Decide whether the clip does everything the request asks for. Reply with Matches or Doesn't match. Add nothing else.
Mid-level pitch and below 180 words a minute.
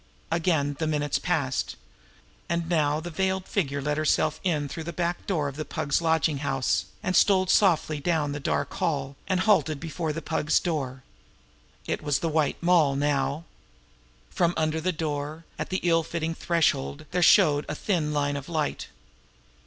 Matches